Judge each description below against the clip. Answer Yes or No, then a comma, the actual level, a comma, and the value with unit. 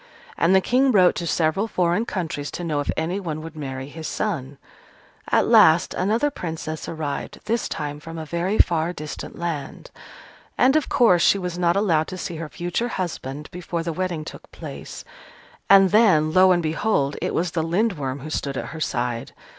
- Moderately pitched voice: Yes, medium, 170 Hz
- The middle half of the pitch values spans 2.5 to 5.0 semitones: Yes, average, 3.3 semitones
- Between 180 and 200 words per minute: Yes, average, 185 wpm